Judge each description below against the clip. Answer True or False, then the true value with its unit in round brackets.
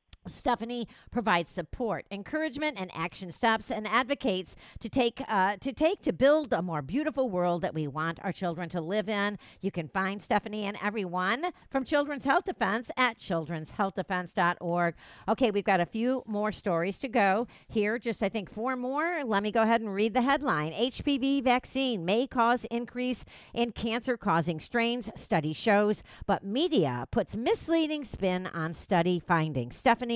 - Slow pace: False (165 wpm)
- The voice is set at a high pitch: True (215 Hz)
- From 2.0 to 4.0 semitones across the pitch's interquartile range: False (5.5 semitones)